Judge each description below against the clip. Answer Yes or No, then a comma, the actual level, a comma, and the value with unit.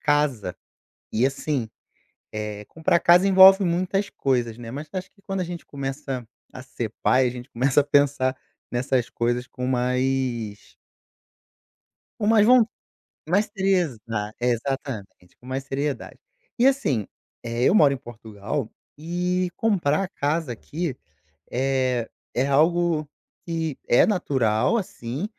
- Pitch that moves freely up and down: Yes, wide, 6.1 semitones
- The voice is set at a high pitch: No, low, 135 Hz